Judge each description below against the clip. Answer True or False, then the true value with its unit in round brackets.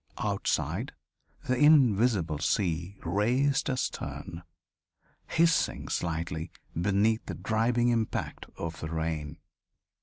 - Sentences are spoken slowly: True (90 wpm)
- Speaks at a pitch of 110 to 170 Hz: False (100 Hz)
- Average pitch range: False (6.7 semitones)